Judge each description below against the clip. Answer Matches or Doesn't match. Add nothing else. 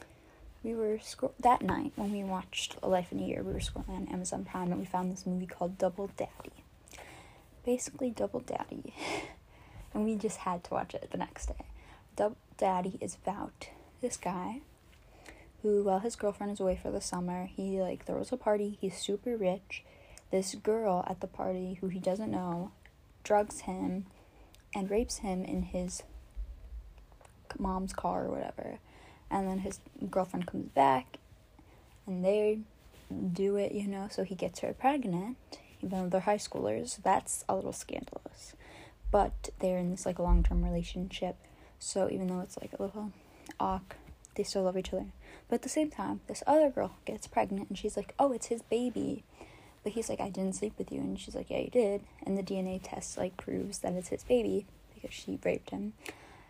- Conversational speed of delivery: Matches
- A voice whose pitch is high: Matches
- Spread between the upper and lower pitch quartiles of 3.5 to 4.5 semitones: Doesn't match